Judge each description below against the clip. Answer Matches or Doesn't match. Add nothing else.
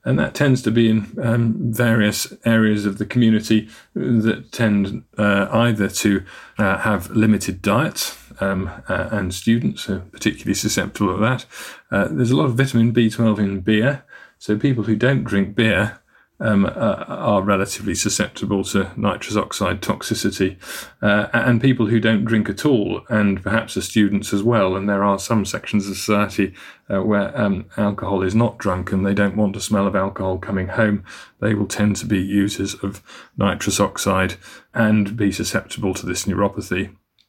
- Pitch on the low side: Matches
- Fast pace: Doesn't match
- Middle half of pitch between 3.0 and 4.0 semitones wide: Doesn't match